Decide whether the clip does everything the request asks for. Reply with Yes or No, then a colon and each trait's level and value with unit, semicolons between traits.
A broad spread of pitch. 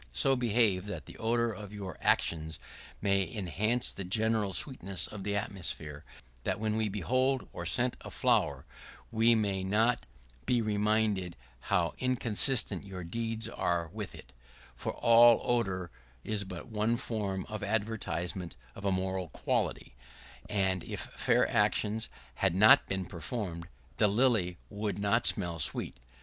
No: average, 3.4 semitones